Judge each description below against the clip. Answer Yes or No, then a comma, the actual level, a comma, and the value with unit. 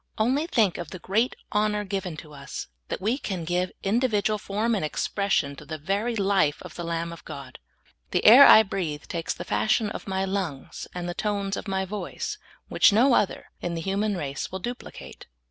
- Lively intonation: No, average, 3.6 semitones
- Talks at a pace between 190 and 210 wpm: Yes, average, 200 wpm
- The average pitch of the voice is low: No, high, 195 Hz